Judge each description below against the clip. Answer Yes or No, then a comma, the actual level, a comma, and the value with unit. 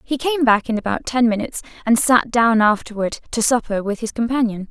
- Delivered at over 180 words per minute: Yes, fast, 205 wpm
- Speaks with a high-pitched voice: Yes, high, 230 Hz